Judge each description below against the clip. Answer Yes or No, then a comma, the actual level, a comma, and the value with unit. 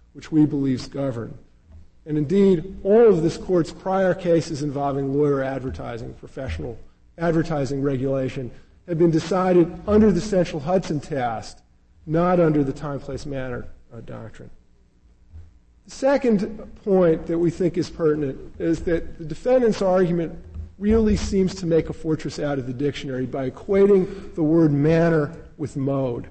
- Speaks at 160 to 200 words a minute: No, average, 145 wpm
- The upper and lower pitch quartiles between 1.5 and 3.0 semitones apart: No, average, 4.9 semitones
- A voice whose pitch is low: No, medium, 155 Hz